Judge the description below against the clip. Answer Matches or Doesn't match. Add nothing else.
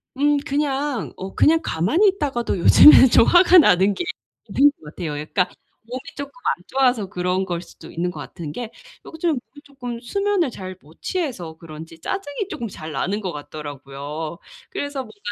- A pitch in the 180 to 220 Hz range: Doesn't match